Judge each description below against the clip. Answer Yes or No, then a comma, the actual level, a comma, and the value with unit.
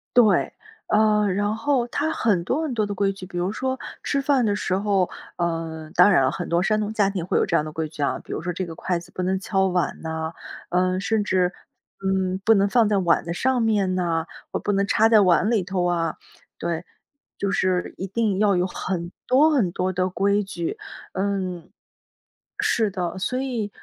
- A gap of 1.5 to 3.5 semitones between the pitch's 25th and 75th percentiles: Yes, average, 3.2 semitones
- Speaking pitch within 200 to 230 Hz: No, high, 190 Hz